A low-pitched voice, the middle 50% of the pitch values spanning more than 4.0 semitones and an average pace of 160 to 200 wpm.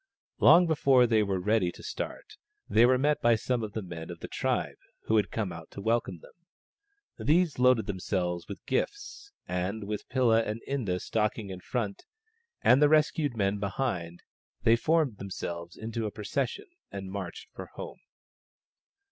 Yes: low, 110 Hz; average, 5.0 semitones; average, 170 wpm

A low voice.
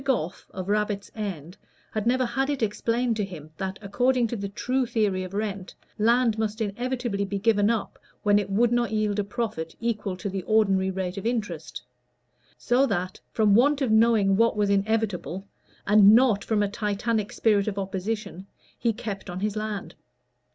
No: high, 210 Hz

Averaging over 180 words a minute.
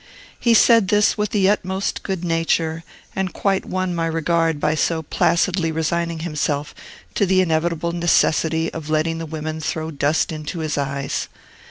No: average, 160 wpm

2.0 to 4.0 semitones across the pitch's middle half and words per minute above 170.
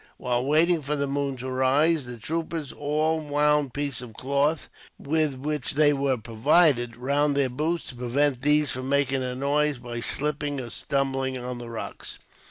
Yes: average, 2.7 semitones; average, 180 wpm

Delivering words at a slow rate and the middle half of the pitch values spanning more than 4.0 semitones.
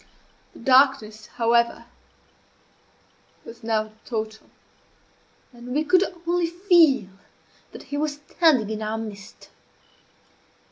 Yes: slow, 100 wpm; wide, 5.4 semitones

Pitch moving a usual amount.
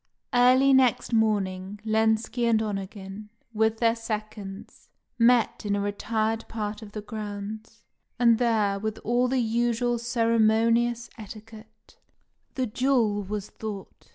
No: narrow, 2.0 semitones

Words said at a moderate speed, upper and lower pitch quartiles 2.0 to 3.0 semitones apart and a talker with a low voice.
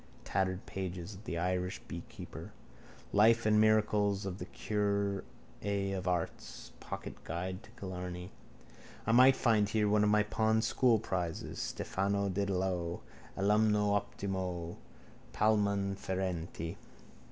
No: slow, 110 wpm; narrow, 2.4 semitones; low, 100 Hz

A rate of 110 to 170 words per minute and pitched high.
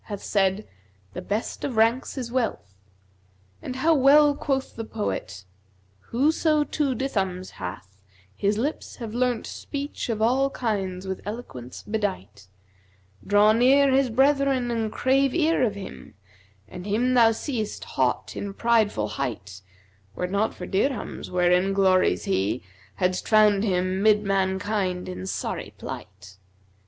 Yes: average, 150 wpm; high, 210 Hz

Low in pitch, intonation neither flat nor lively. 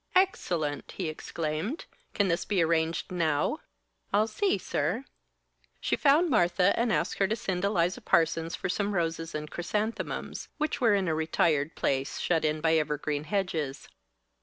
No: medium, 170 Hz; average, 4.6 semitones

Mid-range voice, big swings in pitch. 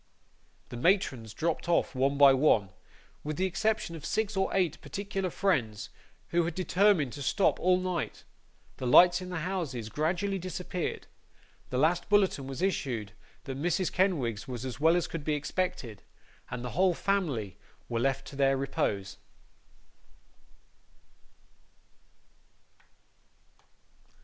Yes: medium, 160 Hz; wide, 5.9 semitones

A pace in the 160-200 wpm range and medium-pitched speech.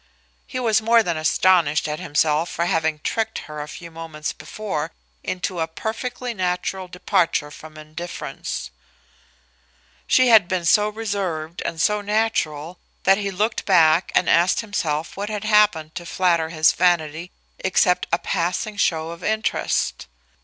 No: average, 145 wpm; medium, 180 Hz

